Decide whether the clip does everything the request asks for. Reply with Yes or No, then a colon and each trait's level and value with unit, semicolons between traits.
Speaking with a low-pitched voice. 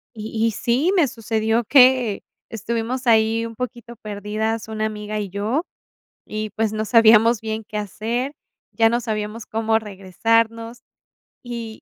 No: high, 225 Hz